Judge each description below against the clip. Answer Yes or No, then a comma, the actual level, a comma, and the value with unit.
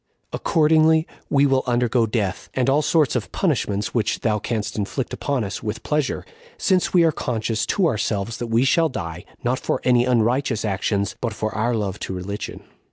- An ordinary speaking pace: Yes, average, 180 wpm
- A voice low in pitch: Yes, low, 120 Hz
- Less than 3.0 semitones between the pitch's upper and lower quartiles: No, average, 4.6 semitones